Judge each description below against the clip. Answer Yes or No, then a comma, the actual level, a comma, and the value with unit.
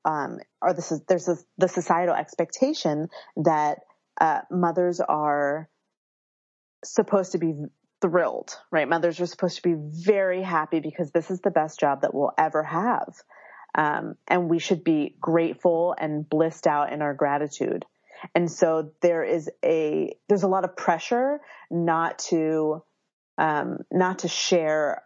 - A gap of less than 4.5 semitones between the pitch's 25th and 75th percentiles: Yes, average, 2.9 semitones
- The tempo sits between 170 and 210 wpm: No, average, 150 wpm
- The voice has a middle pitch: Yes, medium, 170 Hz